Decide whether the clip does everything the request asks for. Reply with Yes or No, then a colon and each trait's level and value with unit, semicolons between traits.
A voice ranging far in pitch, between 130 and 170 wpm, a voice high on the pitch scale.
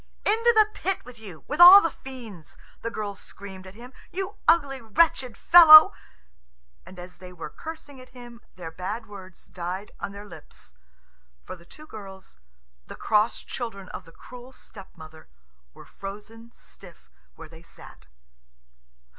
Yes: wide, 6.2 semitones; average, 155 wpm; high, 210 Hz